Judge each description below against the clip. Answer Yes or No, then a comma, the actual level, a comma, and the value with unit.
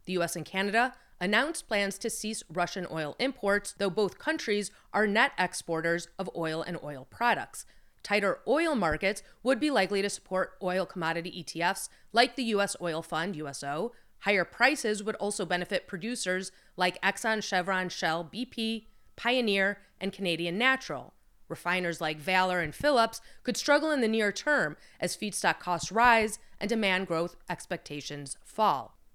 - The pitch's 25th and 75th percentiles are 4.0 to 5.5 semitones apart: Yes, average, 4.3 semitones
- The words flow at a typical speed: Yes, average, 150 wpm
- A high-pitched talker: Yes, high, 195 Hz